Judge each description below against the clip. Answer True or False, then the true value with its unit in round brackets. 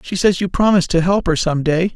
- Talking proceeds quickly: True (275 wpm)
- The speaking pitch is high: False (180 Hz)